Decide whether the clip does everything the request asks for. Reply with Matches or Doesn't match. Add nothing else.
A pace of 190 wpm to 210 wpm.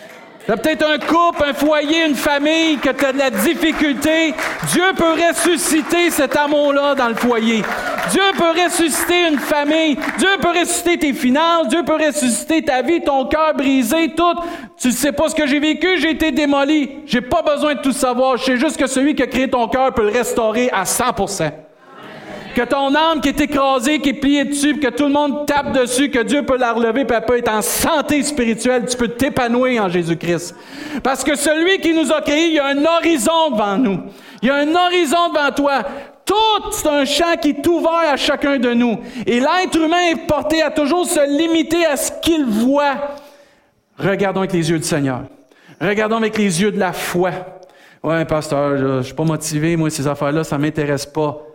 Matches